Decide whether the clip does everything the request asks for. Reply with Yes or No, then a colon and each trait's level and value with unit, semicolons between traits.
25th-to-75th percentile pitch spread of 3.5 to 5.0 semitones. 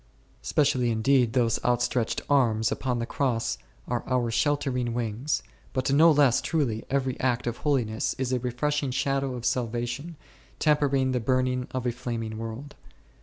No: average, 2.7 semitones